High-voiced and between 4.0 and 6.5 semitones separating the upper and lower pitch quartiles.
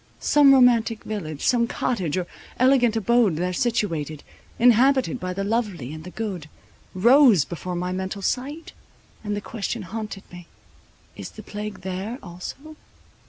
Yes: high, 210 Hz; average, 5.0 semitones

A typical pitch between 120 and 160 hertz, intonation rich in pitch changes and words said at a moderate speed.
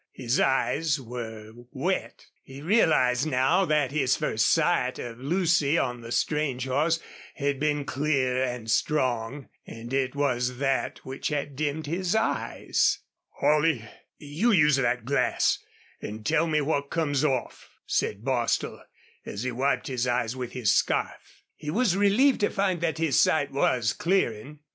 No: medium, 140 Hz; average, 3.8 semitones; average, 150 wpm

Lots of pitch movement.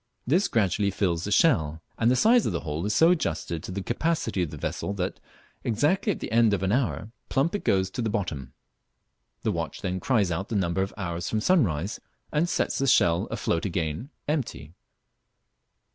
Yes: wide, 6.9 semitones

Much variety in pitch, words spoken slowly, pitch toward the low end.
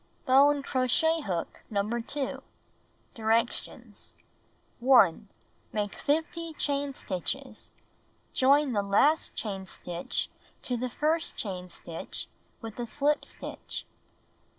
No: wide, 5.9 semitones; slow, 105 wpm; very high, 250 Hz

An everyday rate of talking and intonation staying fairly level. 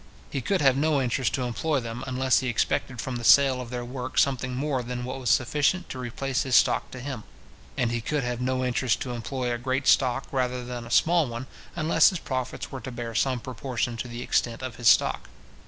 No: fast, 225 wpm; narrow, 1.8 semitones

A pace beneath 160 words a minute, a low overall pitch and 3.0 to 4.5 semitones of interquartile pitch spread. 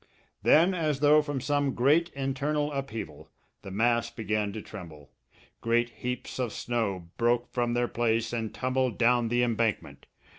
Yes: average, 150 wpm; low, 120 Hz; average, 3.5 semitones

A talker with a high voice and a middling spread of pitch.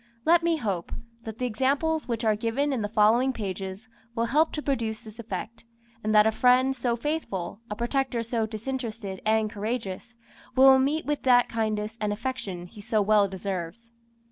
Yes: high, 230 Hz; average, 3.7 semitones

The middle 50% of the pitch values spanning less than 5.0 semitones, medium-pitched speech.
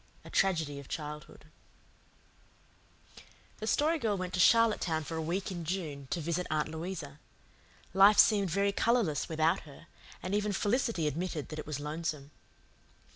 Yes: average, 4.4 semitones; medium, 170 Hz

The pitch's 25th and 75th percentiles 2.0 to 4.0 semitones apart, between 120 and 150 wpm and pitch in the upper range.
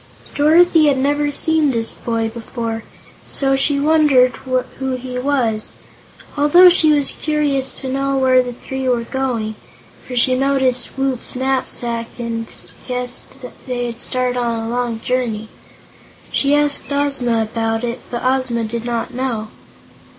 Yes: average, 2.7 semitones; average, 145 wpm; very high, 255 Hz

